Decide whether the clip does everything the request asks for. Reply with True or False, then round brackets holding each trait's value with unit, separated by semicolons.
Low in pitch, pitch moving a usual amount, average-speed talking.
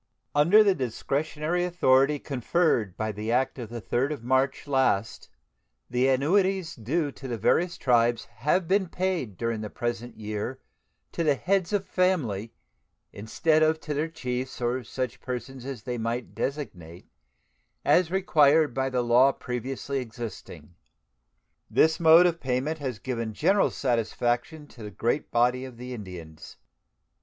True (130 Hz; 5.0 semitones; 150 wpm)